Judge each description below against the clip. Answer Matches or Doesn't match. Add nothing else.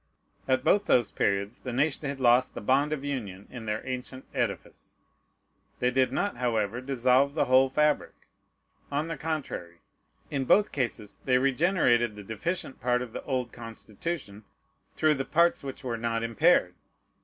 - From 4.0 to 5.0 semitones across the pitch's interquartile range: Doesn't match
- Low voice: Matches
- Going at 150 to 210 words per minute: Matches